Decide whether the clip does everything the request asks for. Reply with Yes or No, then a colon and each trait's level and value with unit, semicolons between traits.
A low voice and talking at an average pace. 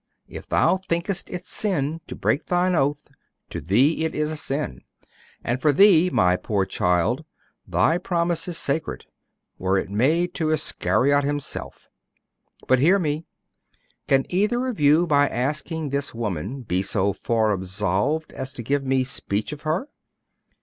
No: medium, 145 Hz; average, 150 wpm